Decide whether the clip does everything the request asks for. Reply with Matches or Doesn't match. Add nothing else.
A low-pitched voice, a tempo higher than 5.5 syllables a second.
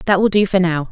Doesn't match